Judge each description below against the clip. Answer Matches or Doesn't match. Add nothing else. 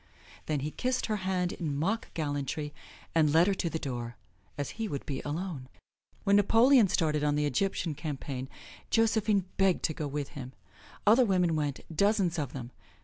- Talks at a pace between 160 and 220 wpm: Matches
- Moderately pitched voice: Matches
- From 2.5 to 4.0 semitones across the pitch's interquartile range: Doesn't match